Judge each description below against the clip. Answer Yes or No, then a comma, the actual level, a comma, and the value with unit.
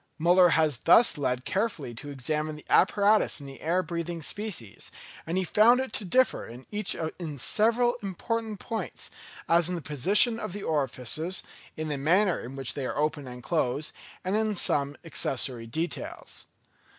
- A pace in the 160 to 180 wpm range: Yes, average, 170 wpm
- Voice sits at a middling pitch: Yes, medium, 165 Hz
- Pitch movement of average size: No, wide, 6.5 semitones